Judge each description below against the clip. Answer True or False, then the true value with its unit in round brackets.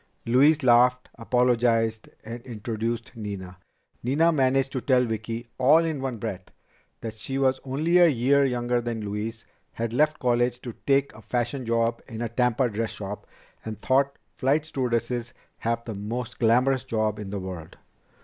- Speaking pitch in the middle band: False (120 Hz)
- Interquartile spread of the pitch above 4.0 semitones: False (2.7 semitones)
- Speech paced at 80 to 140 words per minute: False (160 wpm)